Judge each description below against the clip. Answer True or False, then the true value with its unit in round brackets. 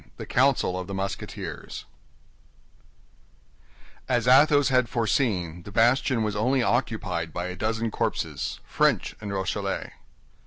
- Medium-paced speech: False (120 wpm)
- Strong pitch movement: False (4.9 semitones)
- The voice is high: False (115 Hz)